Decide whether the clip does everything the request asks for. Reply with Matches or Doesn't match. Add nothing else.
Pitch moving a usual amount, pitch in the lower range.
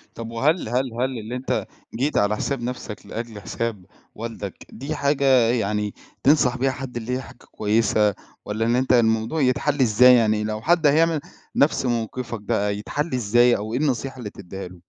Matches